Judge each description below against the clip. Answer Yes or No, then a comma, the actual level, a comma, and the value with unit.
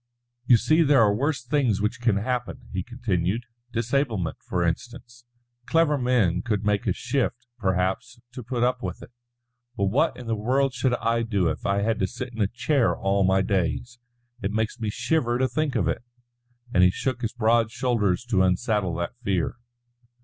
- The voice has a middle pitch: No, low, 115 Hz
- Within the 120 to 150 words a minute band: No, average, 185 wpm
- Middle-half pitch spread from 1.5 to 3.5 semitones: No, average, 4.1 semitones